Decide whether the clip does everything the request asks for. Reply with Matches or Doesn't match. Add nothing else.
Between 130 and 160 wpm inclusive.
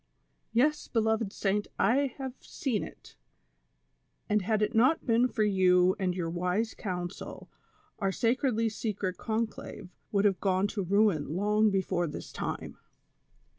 Matches